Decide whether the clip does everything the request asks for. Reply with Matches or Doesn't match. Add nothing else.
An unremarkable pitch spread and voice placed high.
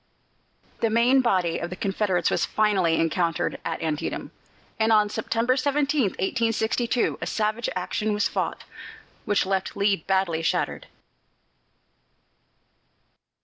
Matches